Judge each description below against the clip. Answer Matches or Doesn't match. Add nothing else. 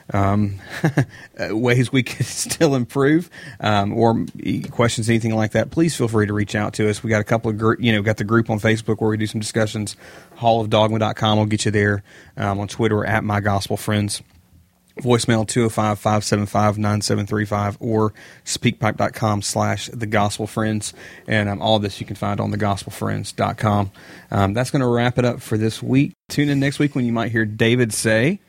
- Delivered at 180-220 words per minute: Matches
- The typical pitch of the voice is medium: Doesn't match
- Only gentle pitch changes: Matches